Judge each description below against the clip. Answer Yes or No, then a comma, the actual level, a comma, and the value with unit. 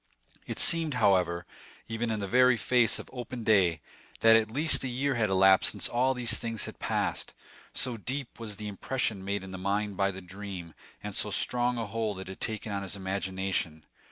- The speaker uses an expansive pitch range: No, average, 3.9 semitones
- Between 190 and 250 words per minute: Yes, average, 200 wpm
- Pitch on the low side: Yes, low, 105 Hz